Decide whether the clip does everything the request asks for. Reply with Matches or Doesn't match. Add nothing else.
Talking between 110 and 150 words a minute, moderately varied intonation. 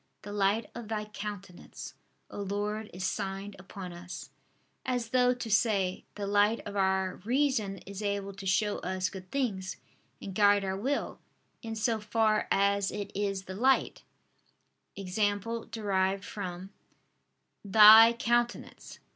Doesn't match